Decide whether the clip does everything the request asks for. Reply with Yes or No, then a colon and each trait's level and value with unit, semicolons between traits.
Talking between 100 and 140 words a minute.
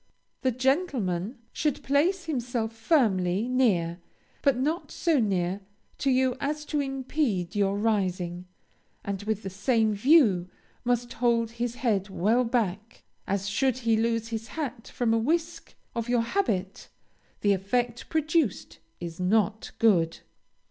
Yes: slow, 135 wpm